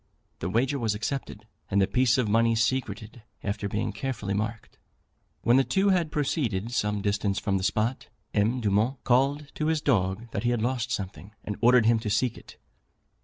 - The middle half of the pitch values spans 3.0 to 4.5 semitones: Yes, average, 3.9 semitones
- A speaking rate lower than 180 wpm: No, average, 185 wpm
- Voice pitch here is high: No, low, 115 Hz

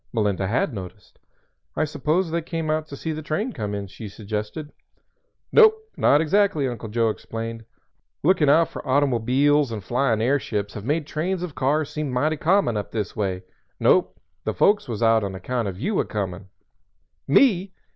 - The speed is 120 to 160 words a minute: No, average, 175 wpm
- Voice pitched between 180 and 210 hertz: No, low, 135 Hz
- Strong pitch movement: Yes, wide, 6.4 semitones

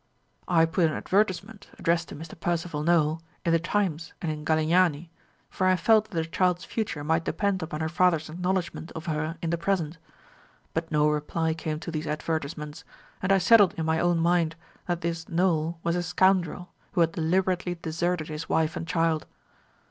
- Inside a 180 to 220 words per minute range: Yes, average, 185 wpm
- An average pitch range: No, narrow, 2.1 semitones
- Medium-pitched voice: Yes, medium, 165 Hz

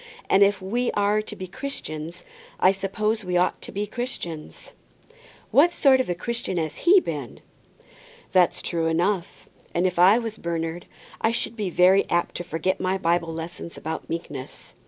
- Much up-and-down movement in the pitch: No, average, 4.0 semitones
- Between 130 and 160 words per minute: No, average, 170 wpm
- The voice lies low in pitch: No, medium, 185 Hz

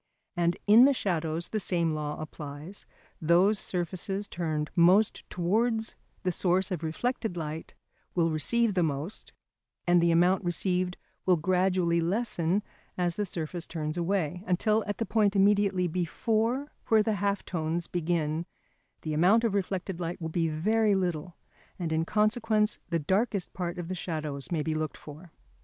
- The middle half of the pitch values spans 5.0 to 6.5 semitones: No, average, 3.7 semitones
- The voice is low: No, medium, 180 Hz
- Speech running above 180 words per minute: No, average, 155 wpm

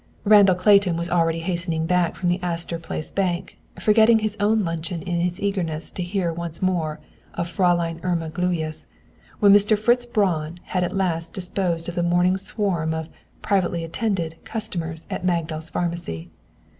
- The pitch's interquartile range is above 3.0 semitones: No, average, 2.7 semitones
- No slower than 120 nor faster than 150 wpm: No, average, 160 wpm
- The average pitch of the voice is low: No, medium, 175 Hz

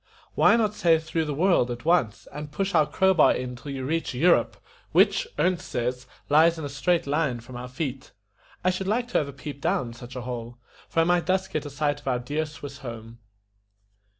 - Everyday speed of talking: No, fast, 225 wpm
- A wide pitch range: No, average, 5.0 semitones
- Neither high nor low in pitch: Yes, medium, 145 Hz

